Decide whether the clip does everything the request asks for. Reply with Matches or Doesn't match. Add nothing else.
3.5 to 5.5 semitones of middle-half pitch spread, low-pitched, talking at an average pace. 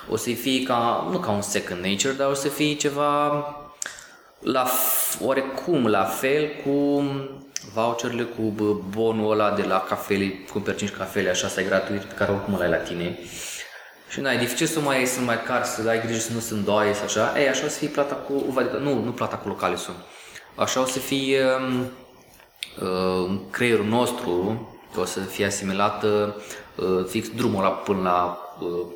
Doesn't match